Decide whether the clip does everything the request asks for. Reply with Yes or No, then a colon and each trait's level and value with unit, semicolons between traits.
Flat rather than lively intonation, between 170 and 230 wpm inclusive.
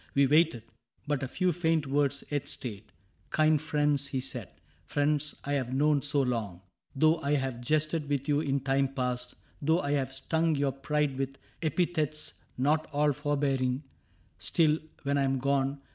Yes: narrow, 2.1 semitones; average, 175 wpm